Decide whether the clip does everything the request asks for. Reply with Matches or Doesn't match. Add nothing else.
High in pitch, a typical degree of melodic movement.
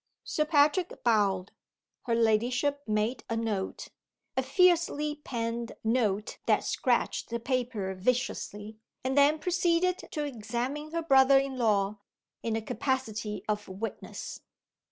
Matches